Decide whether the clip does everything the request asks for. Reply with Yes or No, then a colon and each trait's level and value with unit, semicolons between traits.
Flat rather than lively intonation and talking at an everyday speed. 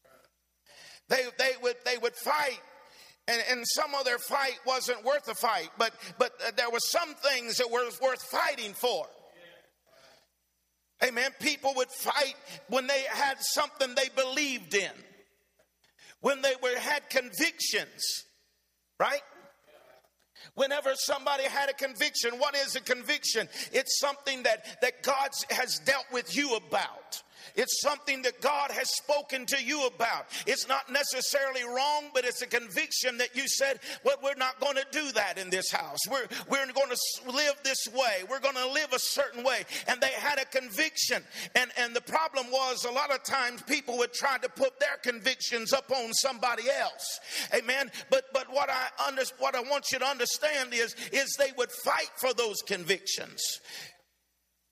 Yes: narrow, 2.3 semitones; average, 170 wpm